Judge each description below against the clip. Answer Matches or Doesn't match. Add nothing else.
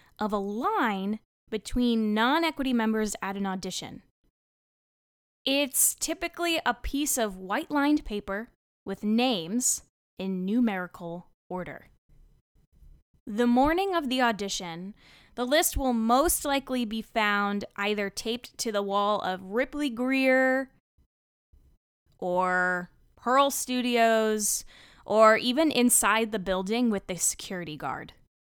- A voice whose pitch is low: Doesn't match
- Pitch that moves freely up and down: Doesn't match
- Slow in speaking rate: Matches